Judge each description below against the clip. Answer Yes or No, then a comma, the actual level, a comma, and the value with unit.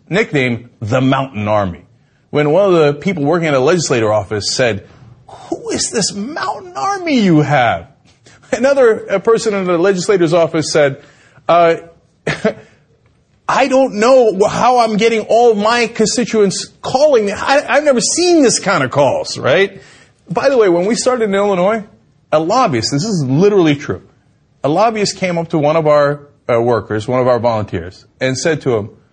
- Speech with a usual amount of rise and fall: No, wide, 8.9 semitones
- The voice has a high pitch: No, medium, 170 Hz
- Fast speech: No, average, 165 wpm